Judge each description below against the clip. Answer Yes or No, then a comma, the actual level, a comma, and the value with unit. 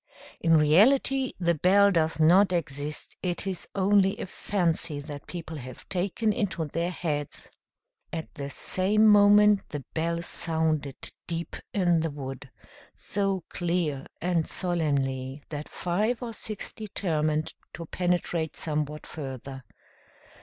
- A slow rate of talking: Yes, slow, 125 wpm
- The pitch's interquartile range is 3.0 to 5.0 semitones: Yes, average, 4.2 semitones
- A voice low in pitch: No, medium, 170 Hz